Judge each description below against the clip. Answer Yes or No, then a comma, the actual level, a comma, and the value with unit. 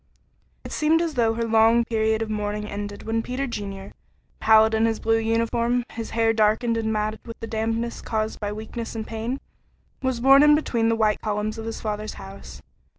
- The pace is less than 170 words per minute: No, average, 195 wpm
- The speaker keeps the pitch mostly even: Yes, narrow, 1.3 semitones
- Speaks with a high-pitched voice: Yes, high, 225 Hz